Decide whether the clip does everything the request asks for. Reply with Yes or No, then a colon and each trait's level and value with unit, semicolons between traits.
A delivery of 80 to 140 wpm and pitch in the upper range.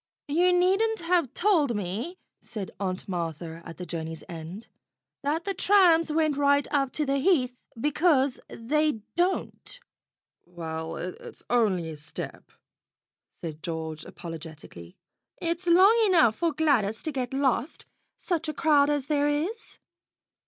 Yes: slow, 135 wpm; very high, 275 Hz